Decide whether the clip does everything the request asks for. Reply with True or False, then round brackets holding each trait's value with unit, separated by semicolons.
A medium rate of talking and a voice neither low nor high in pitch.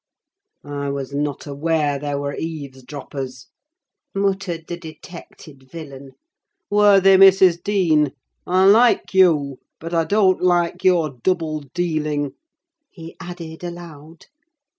False (110 wpm; 165 Hz)